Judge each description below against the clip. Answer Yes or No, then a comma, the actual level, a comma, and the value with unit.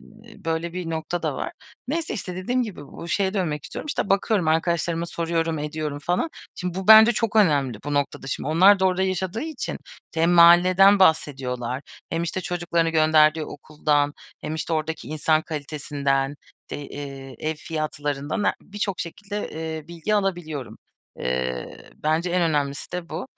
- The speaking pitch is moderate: Yes, medium, 165 Hz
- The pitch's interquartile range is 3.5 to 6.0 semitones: Yes, average, 3.9 semitones